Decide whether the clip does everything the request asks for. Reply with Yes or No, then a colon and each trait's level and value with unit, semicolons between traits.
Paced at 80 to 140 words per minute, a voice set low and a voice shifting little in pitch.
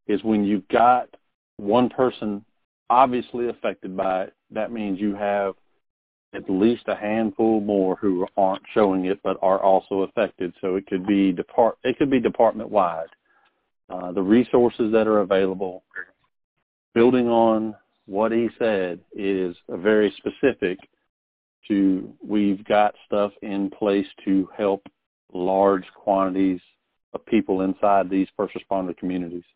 Yes: slow, 135 wpm; low, 100 Hz; narrow, 2.0 semitones